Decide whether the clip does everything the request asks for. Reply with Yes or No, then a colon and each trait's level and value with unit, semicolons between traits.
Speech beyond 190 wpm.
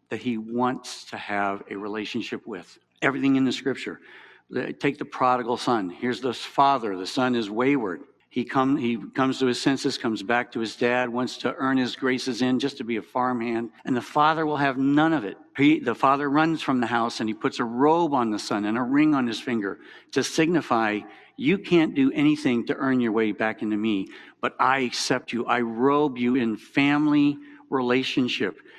Yes: fast, 205 wpm